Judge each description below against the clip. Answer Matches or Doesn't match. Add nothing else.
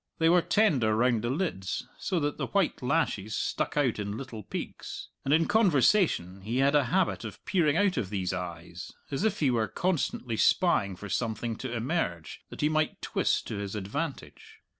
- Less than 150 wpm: Doesn't match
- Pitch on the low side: Matches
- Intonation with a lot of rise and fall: Matches